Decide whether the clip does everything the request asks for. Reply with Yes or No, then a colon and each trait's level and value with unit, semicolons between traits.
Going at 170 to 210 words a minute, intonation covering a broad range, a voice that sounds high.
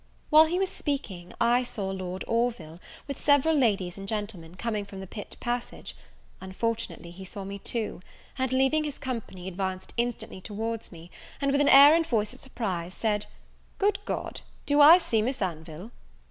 Yes: average, 175 wpm; wide, 5.9 semitones; high, 225 Hz